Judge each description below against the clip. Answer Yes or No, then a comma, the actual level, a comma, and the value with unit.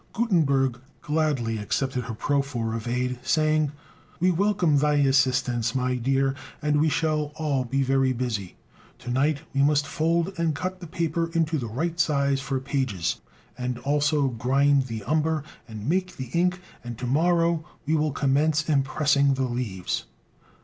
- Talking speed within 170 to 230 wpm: No, average, 155 wpm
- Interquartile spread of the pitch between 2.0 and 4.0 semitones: Yes, average, 3.7 semitones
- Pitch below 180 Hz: Yes, medium, 140 Hz